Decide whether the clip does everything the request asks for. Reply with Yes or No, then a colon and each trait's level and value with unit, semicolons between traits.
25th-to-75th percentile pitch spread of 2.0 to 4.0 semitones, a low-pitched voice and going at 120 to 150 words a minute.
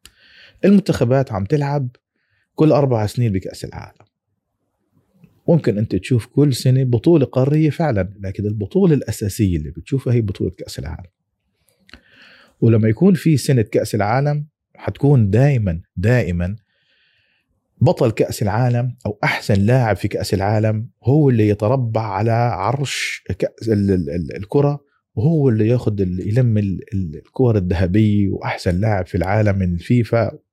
No: average, 4.8 semitones; low, 115 Hz; average, 125 wpm